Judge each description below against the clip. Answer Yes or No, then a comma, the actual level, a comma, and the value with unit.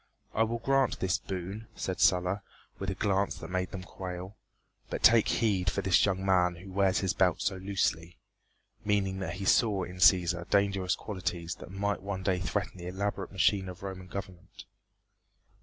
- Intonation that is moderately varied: No, narrow, 1.6 semitones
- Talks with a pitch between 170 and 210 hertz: No, very low, 95 Hz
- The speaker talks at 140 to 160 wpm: No, average, 175 wpm